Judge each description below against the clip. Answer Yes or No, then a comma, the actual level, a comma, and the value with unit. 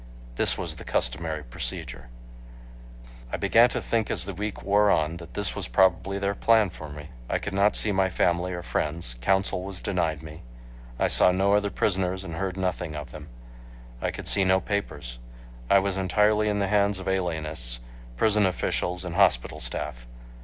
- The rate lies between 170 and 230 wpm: Yes, average, 180 wpm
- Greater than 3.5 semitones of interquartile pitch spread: Yes, average, 4.0 semitones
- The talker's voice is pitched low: Yes, very low, 95 Hz